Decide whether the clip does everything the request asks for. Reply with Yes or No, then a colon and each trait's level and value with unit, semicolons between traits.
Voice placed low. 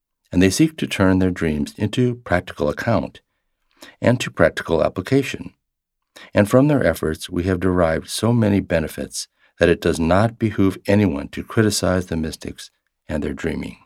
Yes: very low, 95 Hz